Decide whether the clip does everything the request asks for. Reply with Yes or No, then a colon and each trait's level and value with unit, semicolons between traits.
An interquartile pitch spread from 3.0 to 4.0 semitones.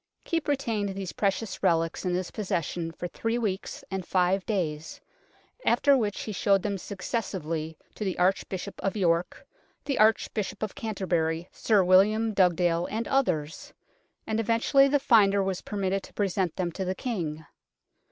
Yes: average, 3.6 semitones